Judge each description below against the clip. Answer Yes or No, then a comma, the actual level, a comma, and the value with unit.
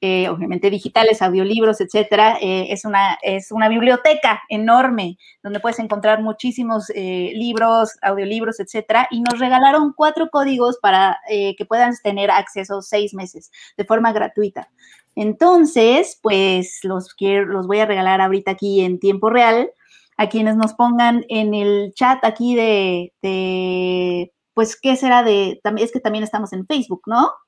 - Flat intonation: No, average, 3.2 semitones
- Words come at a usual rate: Yes, average, 155 wpm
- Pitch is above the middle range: Yes, high, 215 Hz